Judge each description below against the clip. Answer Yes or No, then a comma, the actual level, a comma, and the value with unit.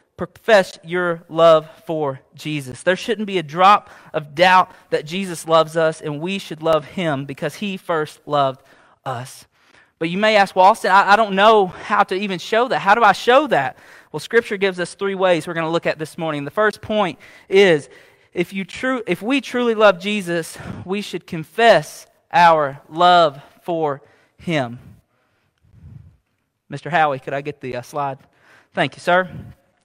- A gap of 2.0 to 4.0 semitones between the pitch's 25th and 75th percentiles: No, average, 5.1 semitones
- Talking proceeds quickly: No, average, 180 wpm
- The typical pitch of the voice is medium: Yes, medium, 170 Hz